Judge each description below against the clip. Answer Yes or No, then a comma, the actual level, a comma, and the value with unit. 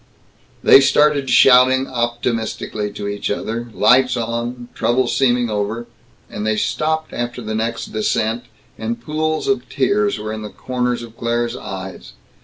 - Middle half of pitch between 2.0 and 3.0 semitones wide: Yes, average, 2.7 semitones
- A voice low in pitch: Yes, low, 120 Hz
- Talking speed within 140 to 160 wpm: Yes, average, 145 wpm